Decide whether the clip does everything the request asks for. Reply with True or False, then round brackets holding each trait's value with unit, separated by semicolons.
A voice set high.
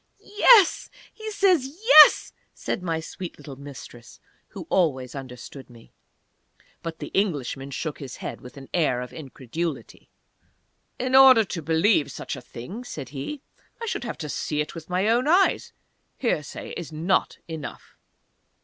False (165 Hz)